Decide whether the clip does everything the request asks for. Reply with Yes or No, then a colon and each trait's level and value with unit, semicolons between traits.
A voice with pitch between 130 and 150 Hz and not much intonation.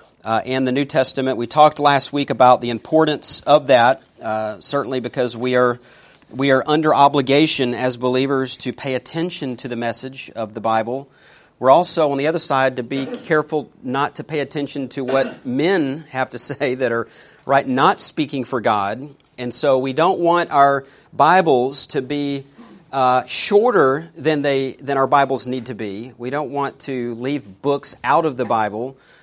Yes: low, 135 Hz; narrow, 2.3 semitones